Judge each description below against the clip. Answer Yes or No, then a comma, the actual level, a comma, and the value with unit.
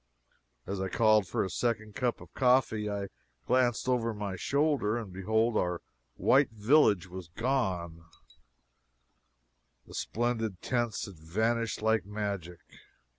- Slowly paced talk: Yes, slow, 125 wpm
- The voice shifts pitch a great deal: No, average, 3.8 semitones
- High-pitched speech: No, low, 110 Hz